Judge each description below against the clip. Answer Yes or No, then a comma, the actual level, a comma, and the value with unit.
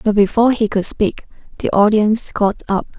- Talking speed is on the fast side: No, average, 180 wpm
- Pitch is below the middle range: No, high, 210 Hz